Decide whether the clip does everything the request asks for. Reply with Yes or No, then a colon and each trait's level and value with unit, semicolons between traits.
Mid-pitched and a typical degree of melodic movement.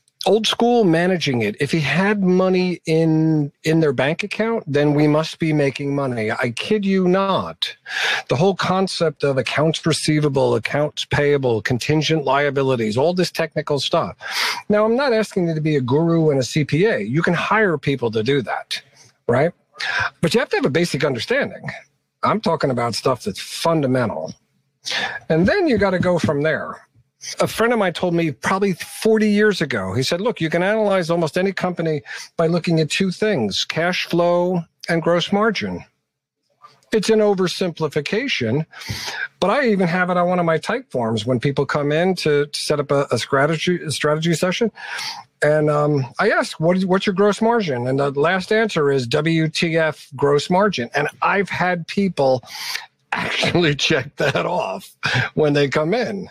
Yes: medium, 165 Hz; average, 4.7 semitones